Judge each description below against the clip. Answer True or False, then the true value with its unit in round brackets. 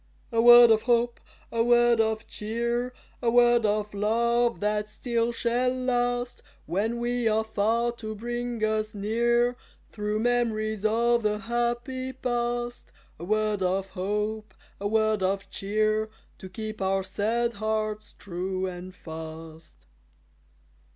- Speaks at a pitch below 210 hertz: False (220 Hz)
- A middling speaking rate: False (130 wpm)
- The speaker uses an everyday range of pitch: False (2.3 semitones)